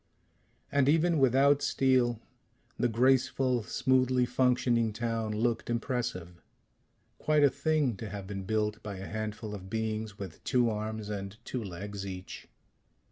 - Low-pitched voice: Yes, low, 115 Hz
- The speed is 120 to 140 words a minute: Yes, slow, 135 wpm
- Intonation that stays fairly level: No, average, 3.7 semitones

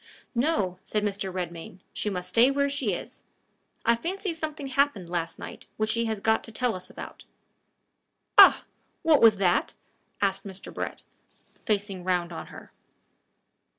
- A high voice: Yes, high, 210 Hz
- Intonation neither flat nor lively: No, wide, 6.0 semitones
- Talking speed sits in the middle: Yes, average, 150 wpm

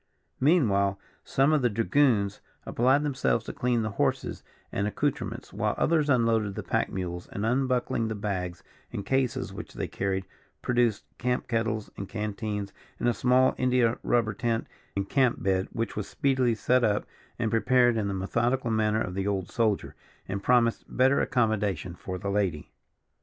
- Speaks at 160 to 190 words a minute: Yes, average, 165 wpm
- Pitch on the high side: No, low, 115 Hz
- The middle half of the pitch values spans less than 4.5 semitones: Yes, average, 3.8 semitones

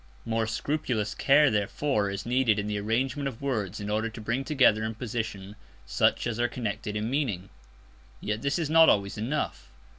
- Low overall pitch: Yes, low, 115 Hz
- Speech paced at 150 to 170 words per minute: No, average, 180 wpm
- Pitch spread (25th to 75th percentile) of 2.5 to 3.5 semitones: No, average, 4.2 semitones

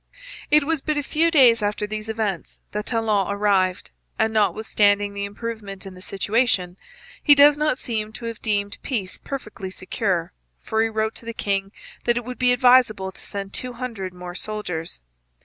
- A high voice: Yes, high, 215 Hz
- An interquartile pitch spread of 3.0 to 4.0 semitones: Yes, average, 3.5 semitones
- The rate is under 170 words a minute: No, average, 180 wpm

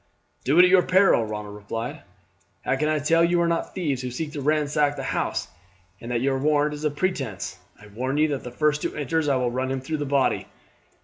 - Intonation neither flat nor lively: Yes, average, 3.5 semitones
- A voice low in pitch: No, medium, 145 Hz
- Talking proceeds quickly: Yes, fast, 235 wpm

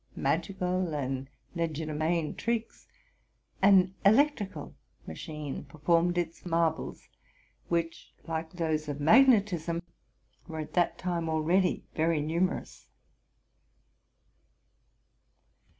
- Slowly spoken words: Yes, slow, 85 wpm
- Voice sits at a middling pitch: Yes, medium, 170 Hz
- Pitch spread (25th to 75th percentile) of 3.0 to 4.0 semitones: No, narrow, 2.6 semitones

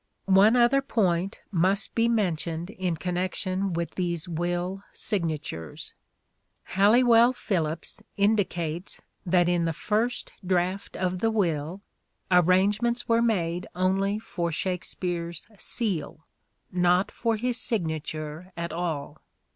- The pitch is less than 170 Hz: No, medium, 185 Hz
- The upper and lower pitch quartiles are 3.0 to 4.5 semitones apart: Yes, average, 3.5 semitones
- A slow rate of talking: Yes, slow, 125 wpm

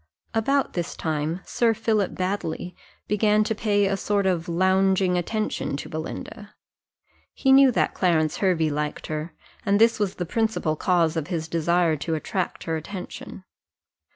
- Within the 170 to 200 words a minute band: No, average, 155 wpm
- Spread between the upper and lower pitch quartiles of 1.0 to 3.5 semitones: No, average, 4.2 semitones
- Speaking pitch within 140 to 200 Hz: Yes, medium, 185 Hz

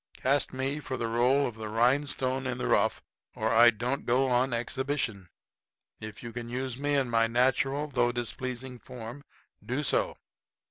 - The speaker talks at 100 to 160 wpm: No, average, 170 wpm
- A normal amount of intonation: No, narrow, 2.1 semitones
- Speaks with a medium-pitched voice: No, low, 125 Hz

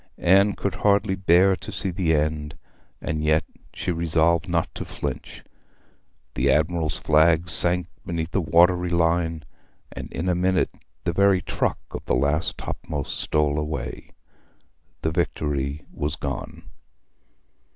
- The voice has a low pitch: Yes, very low, 85 Hz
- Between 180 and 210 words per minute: No, slow, 135 wpm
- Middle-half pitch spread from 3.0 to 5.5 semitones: No, narrow, 2.6 semitones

